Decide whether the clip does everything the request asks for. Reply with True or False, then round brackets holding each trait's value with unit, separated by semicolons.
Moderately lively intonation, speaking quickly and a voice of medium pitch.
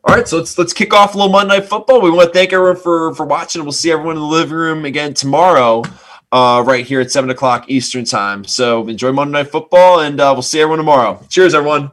True (4.6 semitones; 250 wpm; 155 Hz)